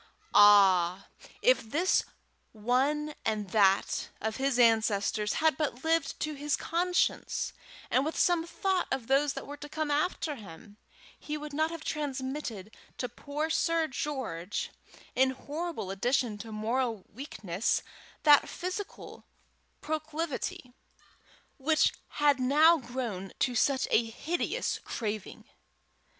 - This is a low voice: No, very high, 270 Hz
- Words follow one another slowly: Yes, slow, 125 wpm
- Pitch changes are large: Yes, wide, 5.8 semitones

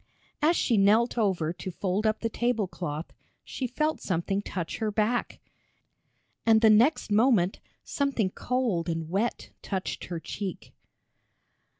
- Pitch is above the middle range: Yes, high, 210 Hz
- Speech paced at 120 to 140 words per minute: Yes, slow, 135 wpm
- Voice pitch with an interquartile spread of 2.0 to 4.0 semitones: No, average, 4.5 semitones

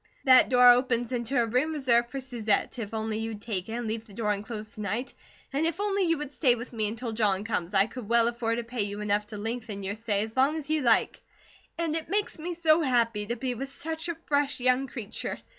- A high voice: Yes, high, 235 Hz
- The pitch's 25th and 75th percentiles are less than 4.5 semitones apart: Yes, average, 3.8 semitones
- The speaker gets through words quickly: Yes, fast, 245 wpm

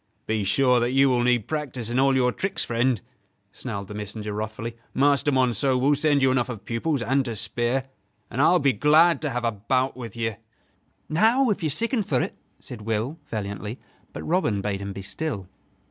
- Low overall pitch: Yes, low, 125 Hz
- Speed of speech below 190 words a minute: No, average, 195 wpm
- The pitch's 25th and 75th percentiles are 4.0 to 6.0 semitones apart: Yes, average, 4.4 semitones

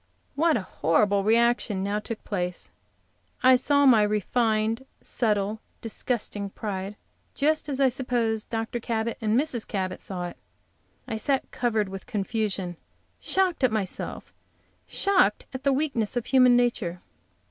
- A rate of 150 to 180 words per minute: No, slow, 135 wpm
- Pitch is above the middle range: Yes, high, 225 Hz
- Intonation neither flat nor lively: Yes, average, 3.7 semitones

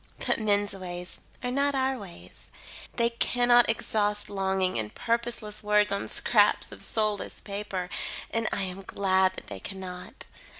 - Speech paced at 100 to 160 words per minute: Yes, average, 145 wpm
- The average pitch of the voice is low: No, high, 205 Hz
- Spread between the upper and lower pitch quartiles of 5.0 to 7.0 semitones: No, average, 3.3 semitones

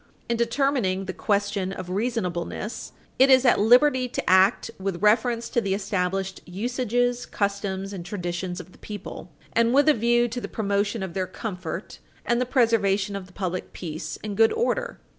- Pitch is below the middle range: No, high, 205 Hz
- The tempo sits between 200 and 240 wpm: No, average, 175 wpm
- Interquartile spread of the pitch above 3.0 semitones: Yes, average, 4.1 semitones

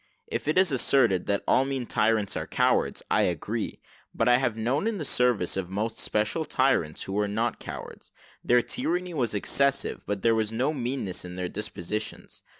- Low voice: Yes, low, 115 Hz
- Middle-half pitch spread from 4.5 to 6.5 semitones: Yes, average, 4.8 semitones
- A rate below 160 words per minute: No, average, 180 wpm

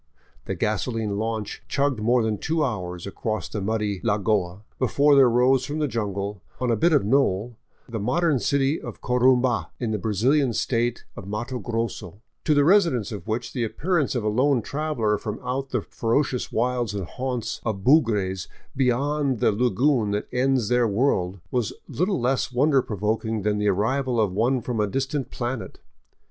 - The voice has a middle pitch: No, low, 120 Hz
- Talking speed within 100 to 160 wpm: No, average, 175 wpm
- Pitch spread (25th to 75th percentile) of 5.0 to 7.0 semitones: No, average, 4.1 semitones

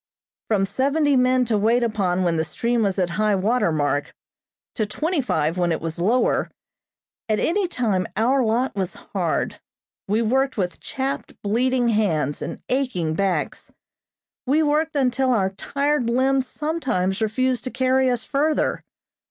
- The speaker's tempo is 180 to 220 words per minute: No, average, 150 wpm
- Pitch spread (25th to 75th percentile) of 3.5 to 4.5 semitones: No, wide, 5.5 semitones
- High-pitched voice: Yes, high, 235 Hz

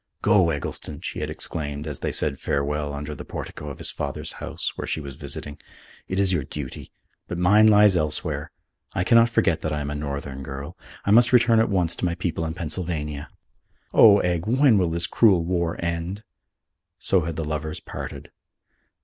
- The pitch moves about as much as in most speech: Yes, average, 4.4 semitones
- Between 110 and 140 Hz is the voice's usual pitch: No, very low, 85 Hz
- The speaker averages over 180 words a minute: Yes, average, 190 wpm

